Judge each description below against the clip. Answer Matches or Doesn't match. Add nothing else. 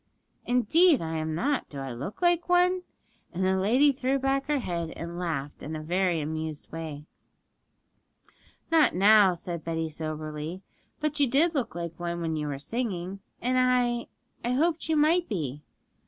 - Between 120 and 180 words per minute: Matches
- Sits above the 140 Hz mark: Matches